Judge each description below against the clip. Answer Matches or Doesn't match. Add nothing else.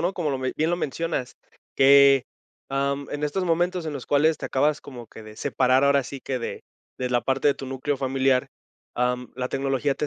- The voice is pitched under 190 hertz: Matches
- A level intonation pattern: Matches